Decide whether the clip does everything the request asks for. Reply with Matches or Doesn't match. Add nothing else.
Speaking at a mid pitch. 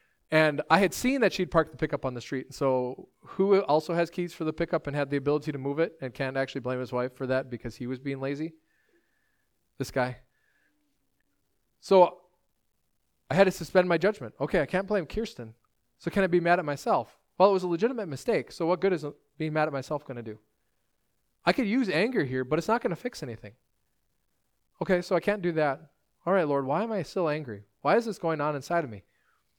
Matches